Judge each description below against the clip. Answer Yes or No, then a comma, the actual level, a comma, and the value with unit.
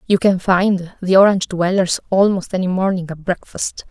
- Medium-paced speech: Yes, average, 170 wpm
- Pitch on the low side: No, medium, 185 Hz